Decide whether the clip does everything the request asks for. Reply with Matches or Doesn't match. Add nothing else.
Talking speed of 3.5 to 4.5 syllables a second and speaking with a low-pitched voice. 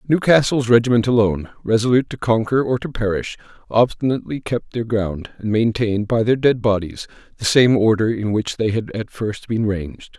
Doesn't match